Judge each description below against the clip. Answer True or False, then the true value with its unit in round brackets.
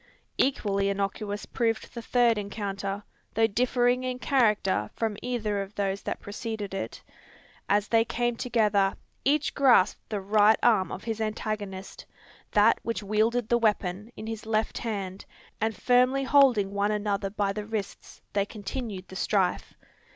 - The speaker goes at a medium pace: True (150 wpm)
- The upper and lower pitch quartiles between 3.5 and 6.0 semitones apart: False (2.8 semitones)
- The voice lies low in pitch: False (215 Hz)